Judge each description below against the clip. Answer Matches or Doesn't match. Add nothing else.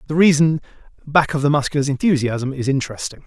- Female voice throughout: Doesn't match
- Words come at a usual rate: Matches